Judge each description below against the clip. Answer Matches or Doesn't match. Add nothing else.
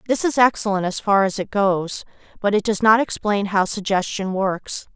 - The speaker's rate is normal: Matches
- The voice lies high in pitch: Matches